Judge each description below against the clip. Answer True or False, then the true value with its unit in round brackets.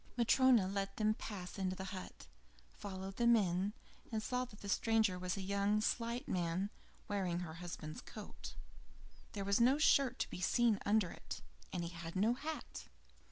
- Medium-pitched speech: False (200 Hz)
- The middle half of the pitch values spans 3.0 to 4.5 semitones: True (3.9 semitones)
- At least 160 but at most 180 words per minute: True (170 wpm)